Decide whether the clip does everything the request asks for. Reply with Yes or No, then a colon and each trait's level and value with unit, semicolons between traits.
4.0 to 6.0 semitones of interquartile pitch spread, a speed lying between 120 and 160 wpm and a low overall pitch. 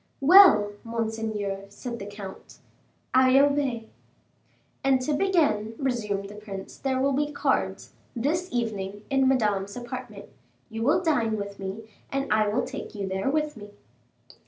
No: average, 4.8 semitones; average, 145 wpm; high, 230 Hz